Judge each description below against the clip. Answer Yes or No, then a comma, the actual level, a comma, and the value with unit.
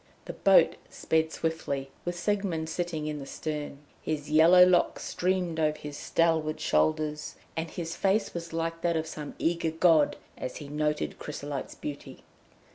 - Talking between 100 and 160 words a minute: Yes, average, 155 wpm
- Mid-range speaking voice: Yes, medium, 160 Hz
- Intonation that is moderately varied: No, narrow, 2.0 semitones